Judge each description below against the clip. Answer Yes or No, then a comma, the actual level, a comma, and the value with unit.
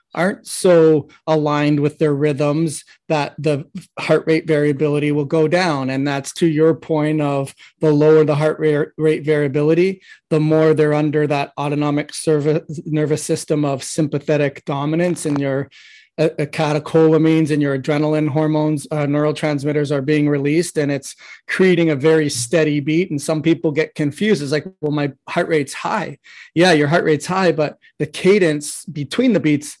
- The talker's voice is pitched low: No, medium, 155 Hz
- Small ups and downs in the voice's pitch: Yes, narrow, 1.3 semitones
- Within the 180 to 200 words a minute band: No, average, 165 wpm